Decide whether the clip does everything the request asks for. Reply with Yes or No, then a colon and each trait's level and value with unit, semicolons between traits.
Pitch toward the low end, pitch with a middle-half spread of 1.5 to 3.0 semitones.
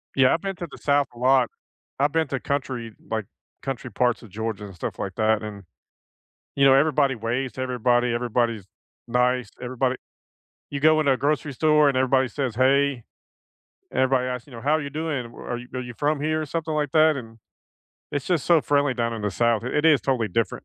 No: low, 130 Hz; average, 3.5 semitones